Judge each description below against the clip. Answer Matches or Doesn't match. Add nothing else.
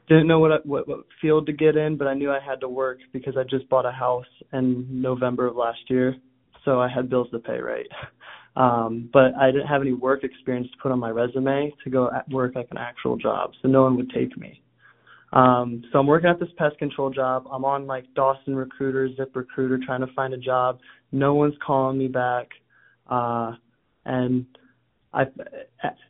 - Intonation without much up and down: Matches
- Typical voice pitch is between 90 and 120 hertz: Doesn't match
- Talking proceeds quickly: Matches